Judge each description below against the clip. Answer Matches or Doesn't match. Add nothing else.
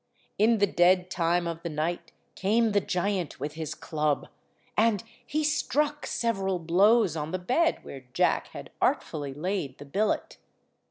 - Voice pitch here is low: Doesn't match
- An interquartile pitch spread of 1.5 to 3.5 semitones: Doesn't match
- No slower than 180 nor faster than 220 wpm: Doesn't match